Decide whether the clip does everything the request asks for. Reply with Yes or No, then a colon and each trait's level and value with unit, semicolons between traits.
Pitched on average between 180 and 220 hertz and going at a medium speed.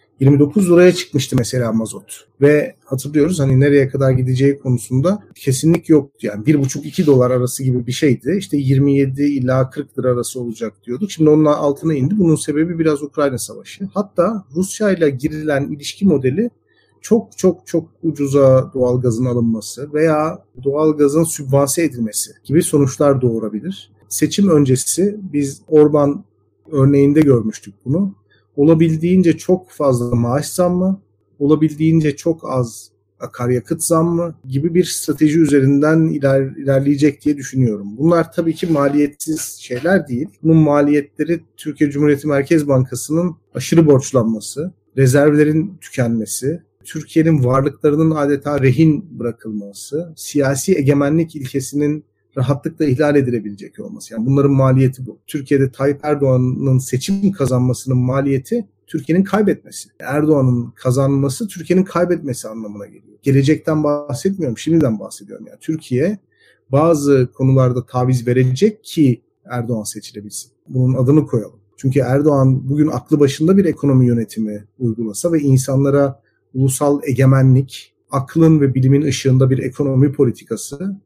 No: medium, 140 Hz; average, 120 wpm